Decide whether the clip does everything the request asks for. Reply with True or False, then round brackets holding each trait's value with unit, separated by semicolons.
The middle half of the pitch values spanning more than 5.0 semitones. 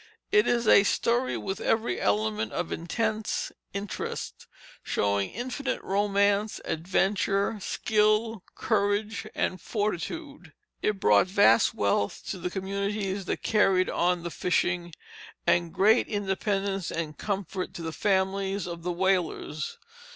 False (3.4 semitones)